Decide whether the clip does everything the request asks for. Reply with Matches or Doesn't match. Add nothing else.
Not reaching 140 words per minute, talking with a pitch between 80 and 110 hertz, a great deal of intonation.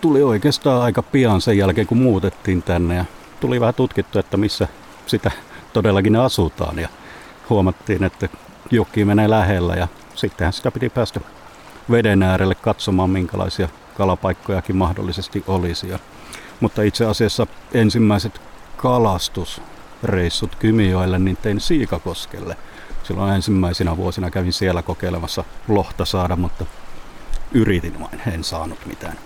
Doesn't match